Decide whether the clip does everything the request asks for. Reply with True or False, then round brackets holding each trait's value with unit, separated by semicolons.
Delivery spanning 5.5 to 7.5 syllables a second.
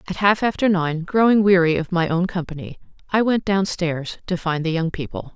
False (5.2 syllables/s)